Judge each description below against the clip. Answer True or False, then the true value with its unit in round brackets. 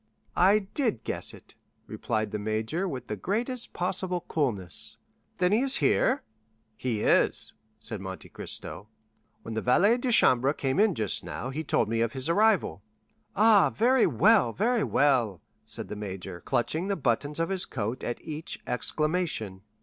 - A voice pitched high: False (140 Hz)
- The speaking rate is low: False (160 wpm)